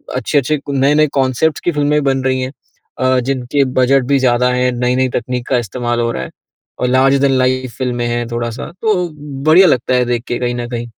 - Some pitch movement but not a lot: No, narrow, 2.1 semitones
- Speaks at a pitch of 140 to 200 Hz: No, low, 130 Hz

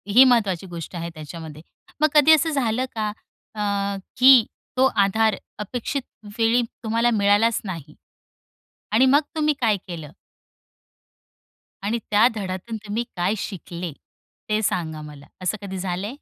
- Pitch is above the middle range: Yes, high, 210 Hz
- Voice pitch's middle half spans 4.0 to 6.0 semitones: Yes, average, 4.9 semitones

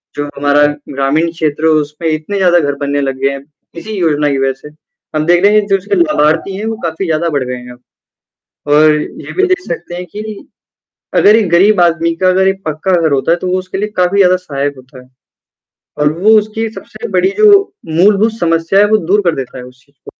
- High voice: No, medium, 170 Hz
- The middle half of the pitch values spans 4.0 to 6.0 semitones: Yes, average, 5.0 semitones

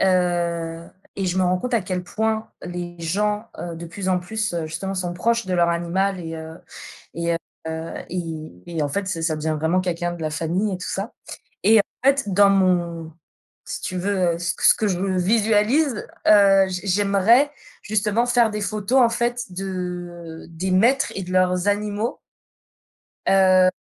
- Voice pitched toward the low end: No, medium, 185 Hz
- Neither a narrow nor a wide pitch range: Yes, average, 3.2 semitones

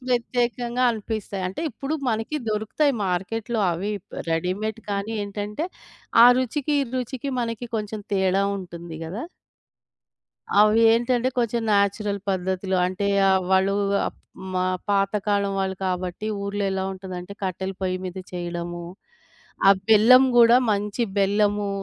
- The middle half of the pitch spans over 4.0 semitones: No, average, 3.2 semitones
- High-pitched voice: Yes, high, 205 Hz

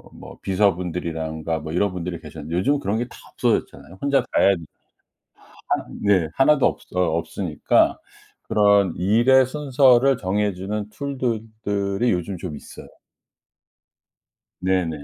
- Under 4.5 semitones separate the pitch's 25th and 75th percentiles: No, wide, 5.4 semitones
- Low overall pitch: Yes, low, 100 Hz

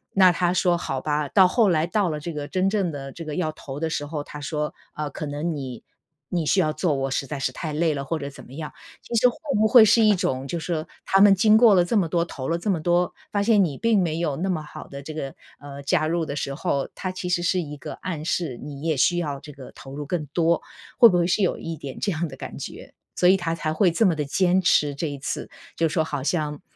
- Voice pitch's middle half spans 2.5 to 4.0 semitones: Yes, average, 3.7 semitones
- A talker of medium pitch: Yes, medium, 160 Hz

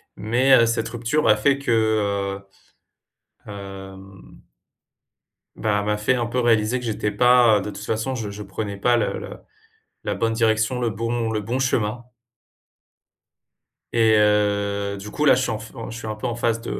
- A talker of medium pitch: No, low, 110 Hz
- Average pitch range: No, narrow, 2.3 semitones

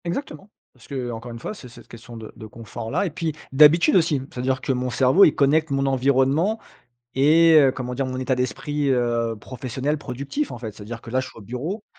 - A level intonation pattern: No, average, 3.8 semitones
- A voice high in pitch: No, low, 130 Hz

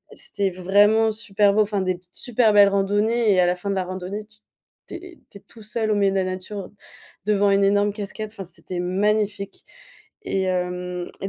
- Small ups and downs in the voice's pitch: Yes, narrow, 2.3 semitones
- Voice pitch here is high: Yes, high, 200 Hz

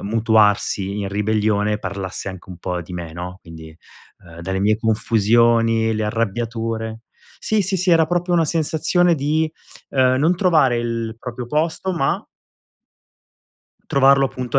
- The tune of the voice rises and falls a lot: Yes, wide, 6.0 semitones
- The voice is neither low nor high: No, low, 115 Hz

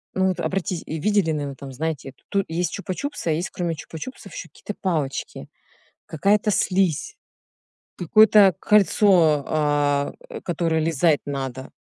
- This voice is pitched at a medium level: Yes, medium, 165 Hz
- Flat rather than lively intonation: No, average, 4.7 semitones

